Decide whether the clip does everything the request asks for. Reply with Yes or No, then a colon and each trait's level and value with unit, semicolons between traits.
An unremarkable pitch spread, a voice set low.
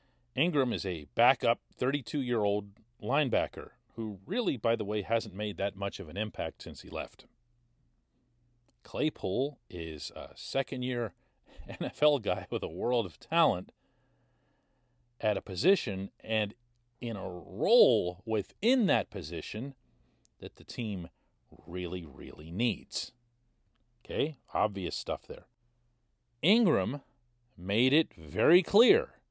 Yes: average, 4.5 semitones; low, 120 Hz